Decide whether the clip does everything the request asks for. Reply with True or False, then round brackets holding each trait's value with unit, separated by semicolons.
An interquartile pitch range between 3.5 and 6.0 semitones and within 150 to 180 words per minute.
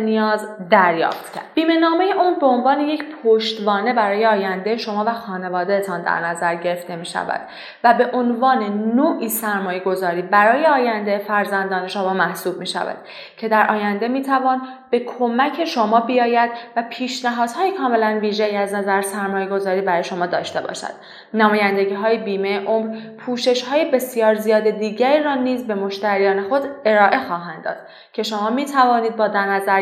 True (3.8 semitones; 155 wpm)